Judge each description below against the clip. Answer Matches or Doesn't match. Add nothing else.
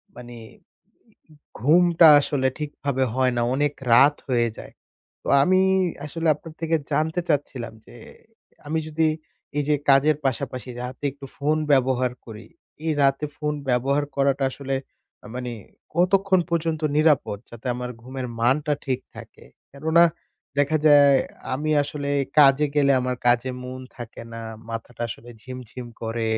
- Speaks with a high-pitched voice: Doesn't match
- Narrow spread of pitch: Doesn't match